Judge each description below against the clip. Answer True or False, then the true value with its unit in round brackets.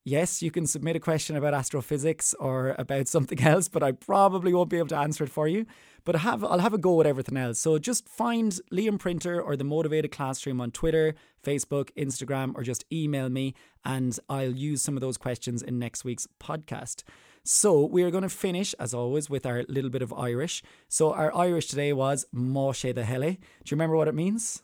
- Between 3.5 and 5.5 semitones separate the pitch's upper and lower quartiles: True (4.1 semitones)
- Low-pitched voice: False (150 Hz)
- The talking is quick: True (215 wpm)